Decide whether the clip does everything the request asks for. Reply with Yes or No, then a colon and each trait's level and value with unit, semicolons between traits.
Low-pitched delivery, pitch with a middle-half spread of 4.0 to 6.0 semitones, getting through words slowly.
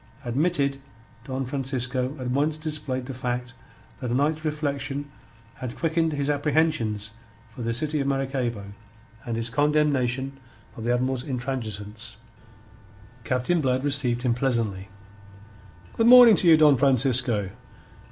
No: low, 130 Hz; average, 3.2 semitones; slow, 130 wpm